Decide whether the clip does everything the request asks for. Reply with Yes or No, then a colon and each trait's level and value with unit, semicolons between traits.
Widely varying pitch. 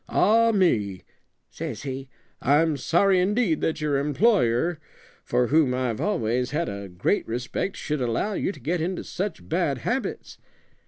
Yes: wide, 7.0 semitones